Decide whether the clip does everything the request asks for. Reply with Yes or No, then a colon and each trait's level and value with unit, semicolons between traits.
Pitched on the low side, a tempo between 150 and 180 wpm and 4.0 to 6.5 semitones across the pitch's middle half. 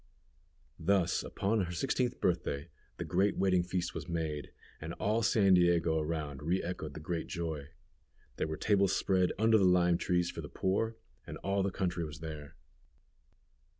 No: very low, 90 Hz; average, 165 wpm; average, 3.3 semitones